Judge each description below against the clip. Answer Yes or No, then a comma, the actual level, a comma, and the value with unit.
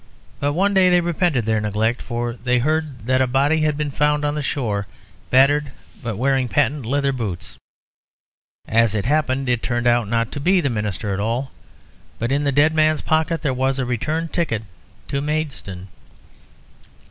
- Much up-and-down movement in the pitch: No, average, 4.3 semitones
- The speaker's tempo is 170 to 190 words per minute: Yes, average, 180 wpm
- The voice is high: No, low, 135 Hz